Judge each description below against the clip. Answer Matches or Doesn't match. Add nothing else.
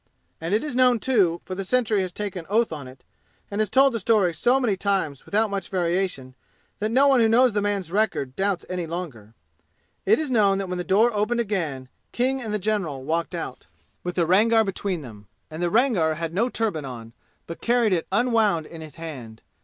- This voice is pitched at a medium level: Doesn't match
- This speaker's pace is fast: Matches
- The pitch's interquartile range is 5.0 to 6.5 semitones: Matches